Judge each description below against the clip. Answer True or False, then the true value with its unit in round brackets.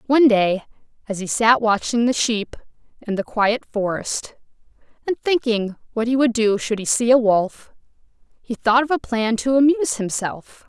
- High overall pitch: True (230 Hz)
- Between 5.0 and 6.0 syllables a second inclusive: False (4.7 syllables/s)